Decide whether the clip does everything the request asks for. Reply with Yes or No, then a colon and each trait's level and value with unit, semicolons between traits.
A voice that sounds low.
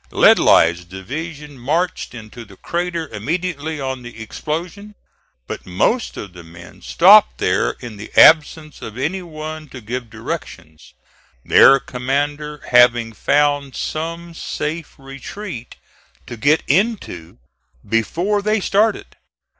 No: medium, 145 Hz